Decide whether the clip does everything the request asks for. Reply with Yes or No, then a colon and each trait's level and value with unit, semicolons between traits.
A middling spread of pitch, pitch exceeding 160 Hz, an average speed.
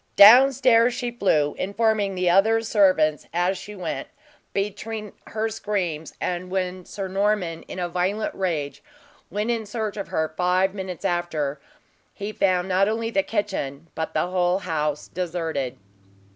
Yes: average, 3.3 semitones; high, 190 Hz; average, 150 wpm